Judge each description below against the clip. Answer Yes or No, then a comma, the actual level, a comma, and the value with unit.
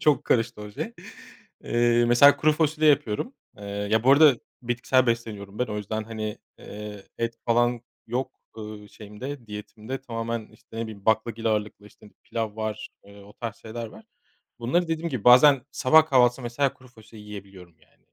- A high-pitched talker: No, low, 115 Hz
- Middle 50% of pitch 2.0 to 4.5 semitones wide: Yes, average, 3.3 semitones